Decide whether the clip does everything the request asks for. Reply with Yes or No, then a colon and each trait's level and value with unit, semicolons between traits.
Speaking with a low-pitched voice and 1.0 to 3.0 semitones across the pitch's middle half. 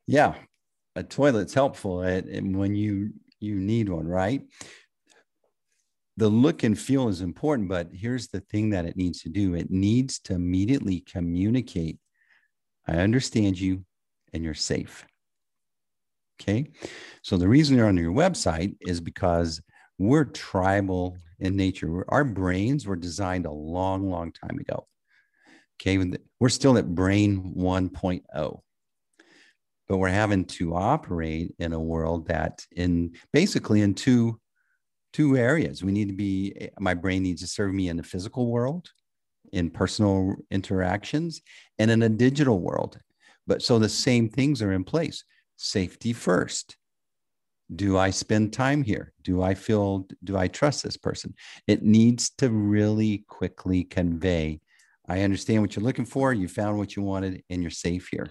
No: very low, 95 Hz; average, 3.8 semitones